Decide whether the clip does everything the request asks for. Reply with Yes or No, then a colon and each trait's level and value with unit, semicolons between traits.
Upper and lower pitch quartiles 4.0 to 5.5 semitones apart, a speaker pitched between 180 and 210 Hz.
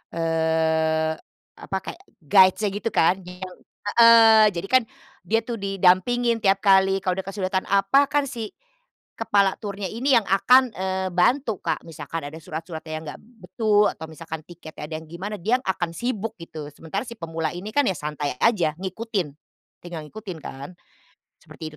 Yes: average, 5.2 semitones; high, 190 Hz